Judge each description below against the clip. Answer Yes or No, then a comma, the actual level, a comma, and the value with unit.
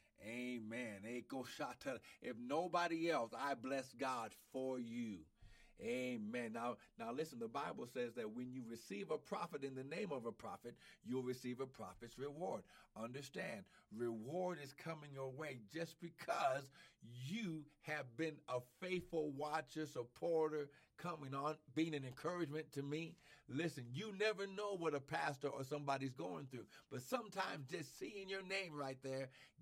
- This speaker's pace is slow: No, average, 150 wpm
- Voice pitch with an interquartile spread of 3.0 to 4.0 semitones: No, average, 5.1 semitones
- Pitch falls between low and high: Yes, medium, 145 Hz